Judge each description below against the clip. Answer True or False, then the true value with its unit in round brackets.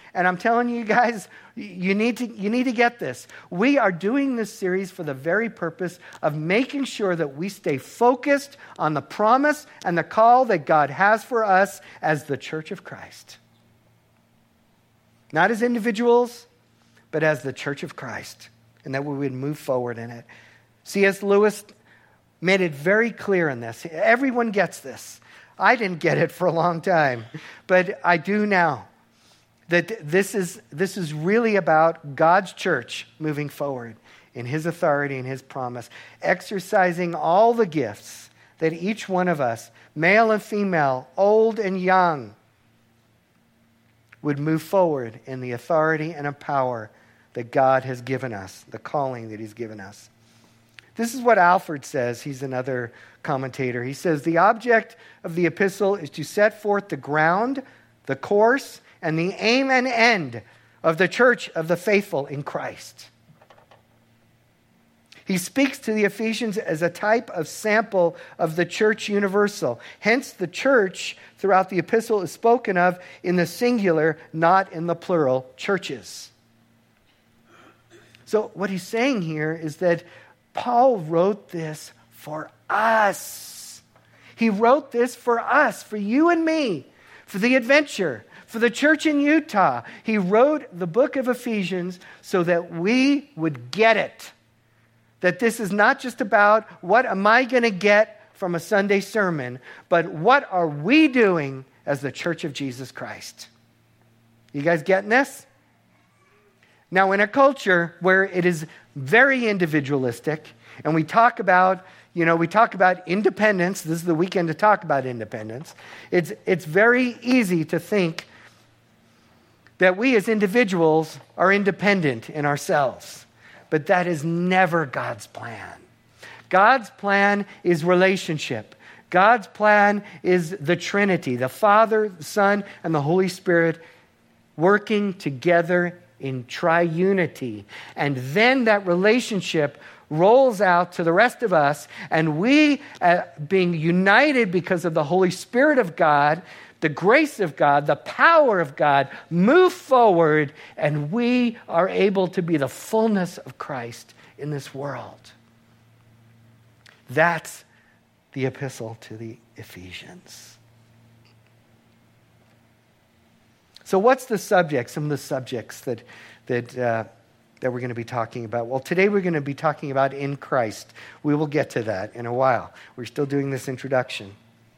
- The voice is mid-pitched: True (170 Hz)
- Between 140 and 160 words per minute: True (150 wpm)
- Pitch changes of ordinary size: False (7.8 semitones)